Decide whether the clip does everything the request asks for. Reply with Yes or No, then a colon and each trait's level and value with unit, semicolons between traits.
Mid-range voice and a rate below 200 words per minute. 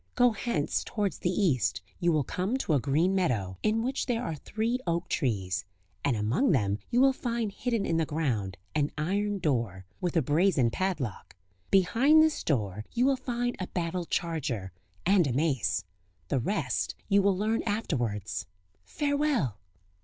Yes: medium, 175 Hz; average, 165 wpm